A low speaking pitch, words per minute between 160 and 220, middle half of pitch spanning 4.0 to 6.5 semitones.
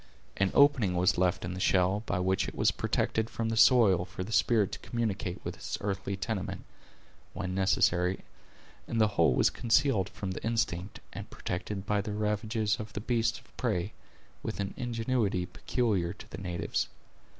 No: low, 100 Hz; average, 175 wpm; average, 3.3 semitones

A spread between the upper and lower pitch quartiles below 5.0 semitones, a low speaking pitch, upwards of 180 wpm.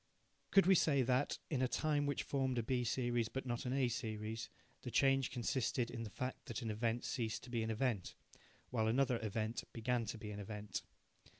Yes: average, 2.9 semitones; low, 120 Hz; fast, 205 wpm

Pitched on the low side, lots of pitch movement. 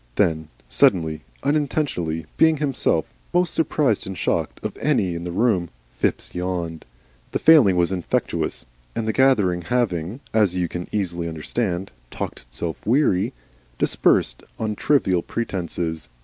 Yes: very low, 95 Hz; wide, 6.1 semitones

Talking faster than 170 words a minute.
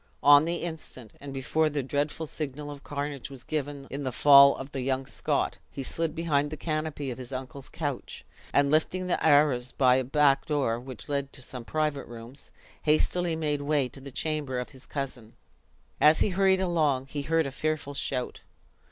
Yes: average, 190 wpm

